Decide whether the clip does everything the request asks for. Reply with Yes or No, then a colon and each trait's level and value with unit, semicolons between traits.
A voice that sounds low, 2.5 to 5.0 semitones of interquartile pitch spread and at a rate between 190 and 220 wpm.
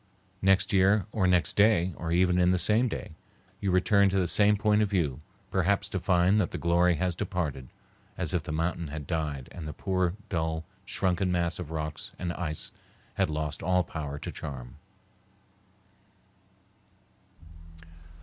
No: very low, 90 Hz; average, 3.1 semitones; average, 160 wpm